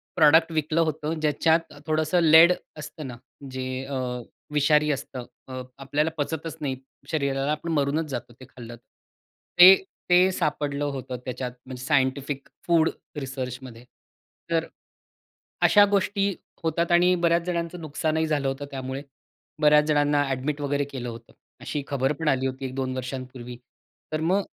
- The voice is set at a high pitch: No, medium, 145 Hz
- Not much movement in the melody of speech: No, average, 3.4 semitones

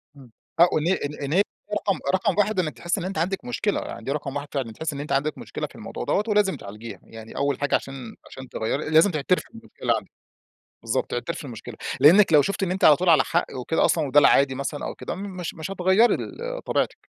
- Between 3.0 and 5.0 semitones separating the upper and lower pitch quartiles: No, wide, 5.5 semitones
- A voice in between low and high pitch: Yes, medium, 160 Hz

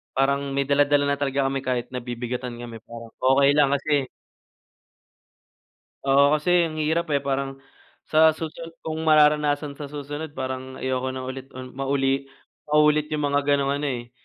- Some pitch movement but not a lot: No, narrow, 2.2 semitones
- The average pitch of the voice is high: No, medium, 140 Hz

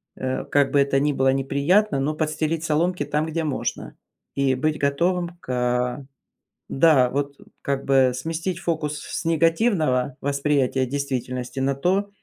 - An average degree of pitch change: Yes, average, 3.5 semitones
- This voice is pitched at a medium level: Yes, medium, 145 Hz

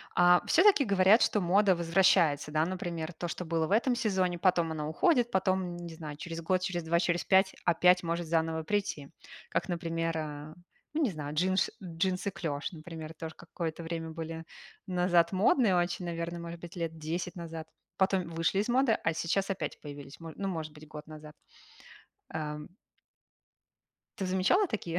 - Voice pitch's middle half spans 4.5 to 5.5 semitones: No, average, 2.7 semitones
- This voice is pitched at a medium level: Yes, medium, 170 Hz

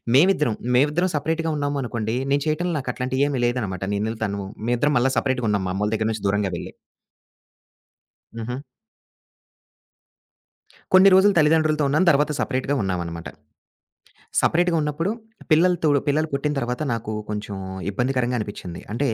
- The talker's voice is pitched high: No, low, 130 Hz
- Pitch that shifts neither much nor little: No, wide, 5.8 semitones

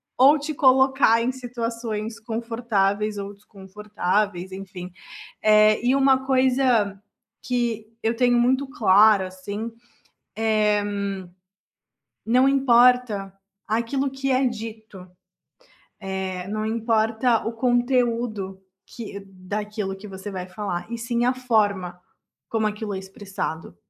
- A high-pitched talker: Yes, high, 220 Hz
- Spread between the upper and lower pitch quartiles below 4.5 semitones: Yes, average, 3.4 semitones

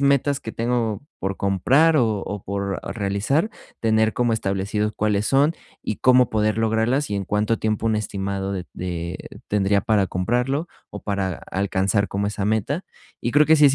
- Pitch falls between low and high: No, low, 105 Hz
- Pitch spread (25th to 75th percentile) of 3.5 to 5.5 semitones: Yes, average, 3.8 semitones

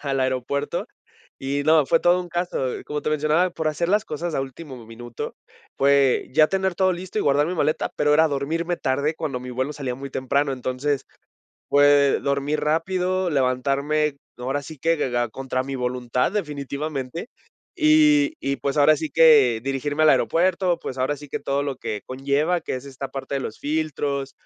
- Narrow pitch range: No, average, 3.2 semitones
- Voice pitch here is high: No, medium, 145 Hz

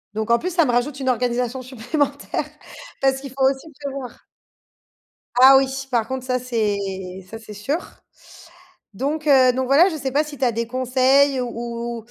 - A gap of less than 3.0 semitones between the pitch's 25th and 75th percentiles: Yes, narrow, 2.5 semitones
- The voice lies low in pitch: No, very high, 260 Hz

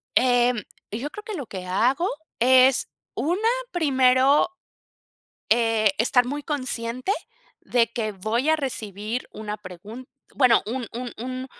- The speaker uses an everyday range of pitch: Yes, average, 3.2 semitones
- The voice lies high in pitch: Yes, high, 245 Hz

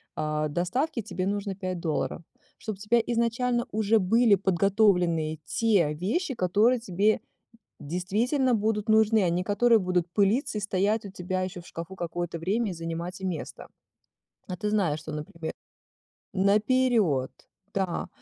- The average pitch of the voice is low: No, high, 195 Hz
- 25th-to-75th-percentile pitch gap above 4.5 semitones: No, average, 4.0 semitones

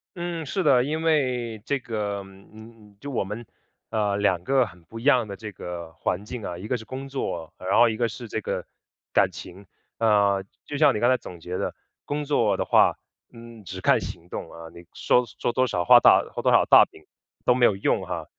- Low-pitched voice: Yes, low, 110 Hz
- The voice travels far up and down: No, average, 4.5 semitones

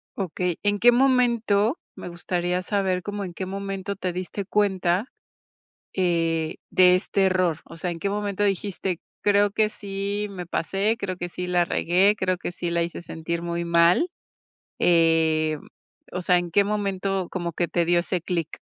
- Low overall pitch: No, medium, 185 Hz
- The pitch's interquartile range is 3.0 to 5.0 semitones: No, narrow, 2.6 semitones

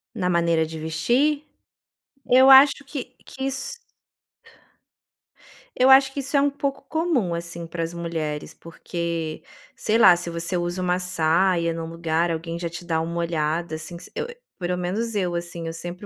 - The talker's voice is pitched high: No, medium, 175 Hz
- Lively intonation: Yes, wide, 6.0 semitones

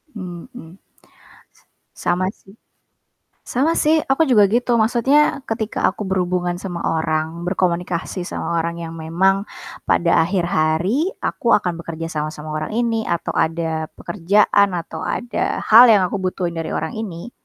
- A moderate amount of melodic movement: Yes, average, 4.7 semitones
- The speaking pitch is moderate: Yes, medium, 180 Hz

